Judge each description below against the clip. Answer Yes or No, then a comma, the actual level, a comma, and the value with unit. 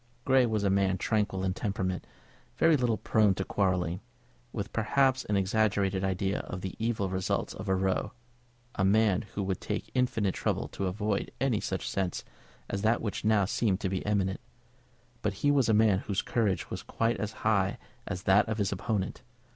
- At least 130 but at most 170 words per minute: No, average, 185 wpm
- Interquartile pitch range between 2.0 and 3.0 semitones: Yes, narrow, 2.5 semitones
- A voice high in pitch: No, low, 100 Hz